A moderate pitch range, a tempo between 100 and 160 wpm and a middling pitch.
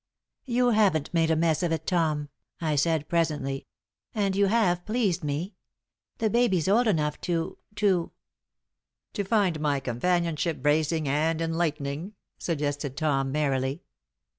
Yes: average, 4.0 semitones; average, 140 wpm; medium, 165 Hz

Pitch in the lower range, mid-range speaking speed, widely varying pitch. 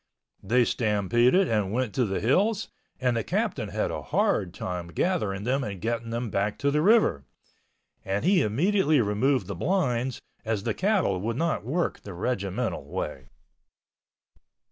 Yes: low, 115 Hz; average, 155 wpm; wide, 6.4 semitones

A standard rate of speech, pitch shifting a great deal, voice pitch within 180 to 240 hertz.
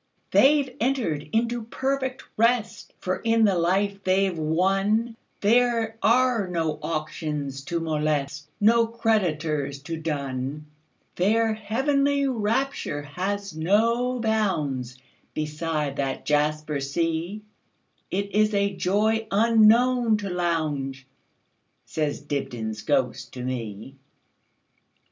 No: slow, 90 wpm; wide, 7.0 semitones; medium, 185 Hz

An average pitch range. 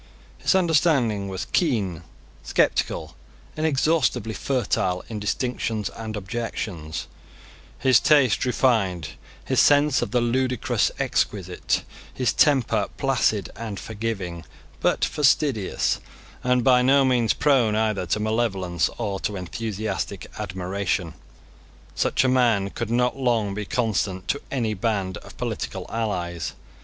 Yes: average, 4.6 semitones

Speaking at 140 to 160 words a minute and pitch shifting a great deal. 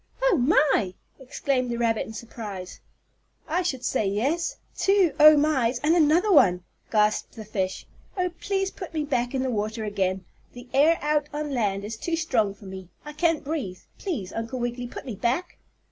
No: average, 180 wpm; wide, 6.4 semitones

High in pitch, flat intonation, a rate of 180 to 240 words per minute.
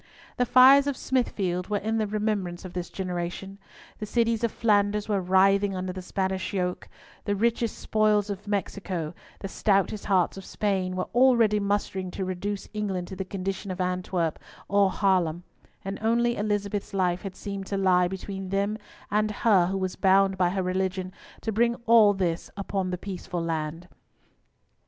No: high, 195 Hz; narrow, 2.3 semitones; average, 170 wpm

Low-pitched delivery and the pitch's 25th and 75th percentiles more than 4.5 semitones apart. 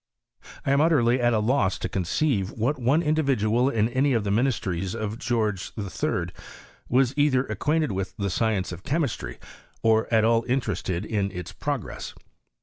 Yes: low, 115 Hz; average, 5.0 semitones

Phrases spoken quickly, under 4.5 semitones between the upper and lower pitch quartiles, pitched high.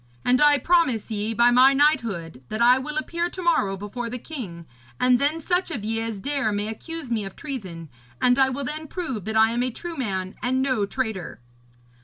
No: fast, 210 wpm; average, 5.2 semitones; high, 245 Hz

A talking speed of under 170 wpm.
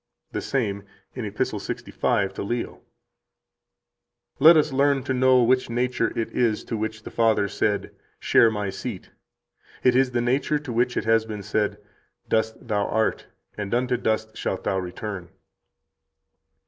Yes: average, 160 wpm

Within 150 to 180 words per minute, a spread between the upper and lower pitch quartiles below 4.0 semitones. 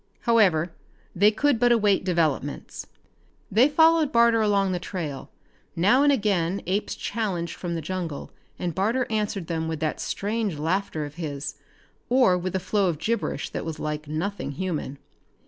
No: average, 160 wpm; average, 5.1 semitones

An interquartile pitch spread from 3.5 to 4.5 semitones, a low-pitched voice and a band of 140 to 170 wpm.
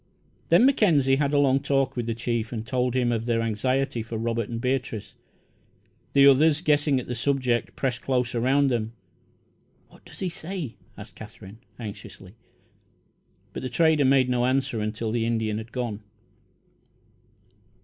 No: average, 3.1 semitones; low, 125 Hz; average, 160 wpm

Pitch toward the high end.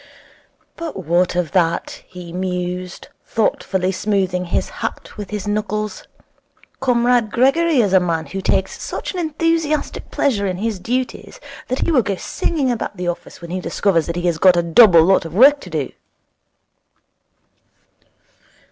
Yes: high, 195 Hz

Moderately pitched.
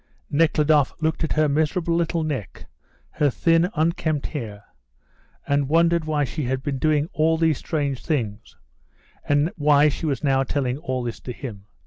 Yes: medium, 150 Hz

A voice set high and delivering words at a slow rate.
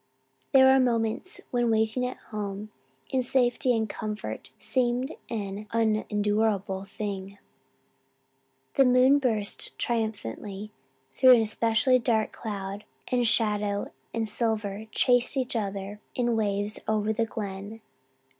Yes: high, 220 Hz; slow, 115 wpm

